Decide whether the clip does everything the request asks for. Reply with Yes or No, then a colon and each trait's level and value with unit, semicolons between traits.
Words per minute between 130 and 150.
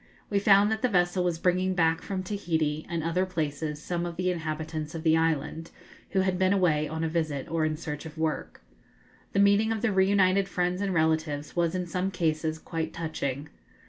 No: average, 200 wpm